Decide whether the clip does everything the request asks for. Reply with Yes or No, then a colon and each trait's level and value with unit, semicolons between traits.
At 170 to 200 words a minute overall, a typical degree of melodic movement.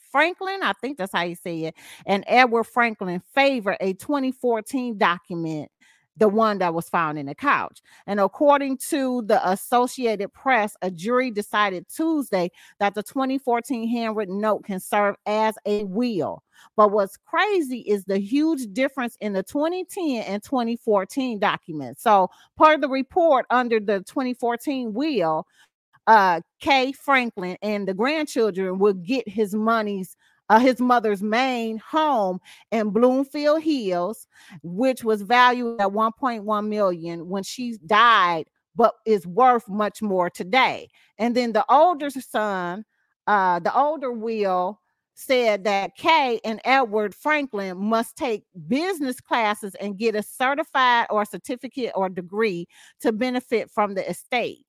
No: average, 145 wpm; average, 4.6 semitones